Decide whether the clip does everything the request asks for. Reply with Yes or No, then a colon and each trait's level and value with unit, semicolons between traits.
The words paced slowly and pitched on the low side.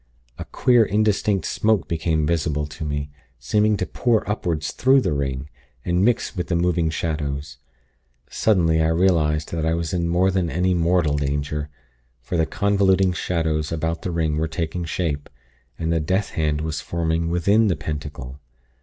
No: average, 165 wpm; very low, 80 Hz